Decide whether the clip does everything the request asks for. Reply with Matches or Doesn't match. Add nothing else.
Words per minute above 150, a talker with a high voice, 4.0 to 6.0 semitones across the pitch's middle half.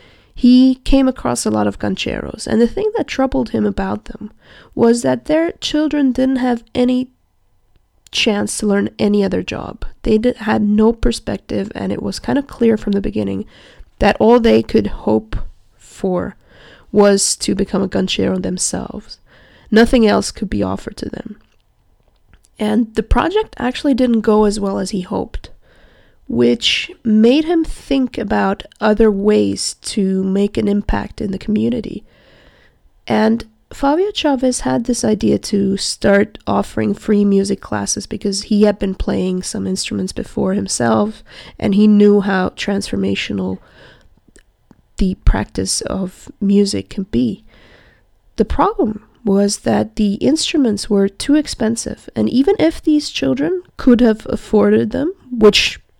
Doesn't match